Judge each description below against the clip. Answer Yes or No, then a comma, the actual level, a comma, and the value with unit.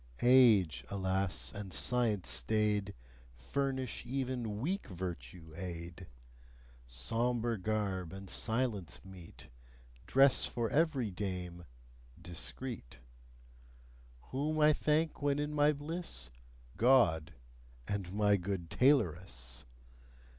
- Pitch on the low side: Yes, low, 105 Hz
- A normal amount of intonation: No, wide, 6.8 semitones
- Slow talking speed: Yes, slow, 95 wpm